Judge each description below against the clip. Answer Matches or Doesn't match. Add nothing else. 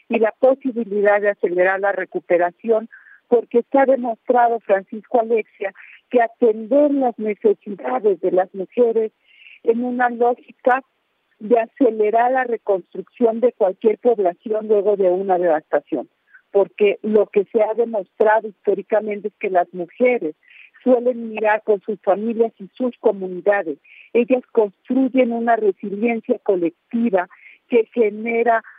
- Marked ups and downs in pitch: Doesn't match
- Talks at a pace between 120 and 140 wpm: Matches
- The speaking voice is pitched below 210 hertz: Doesn't match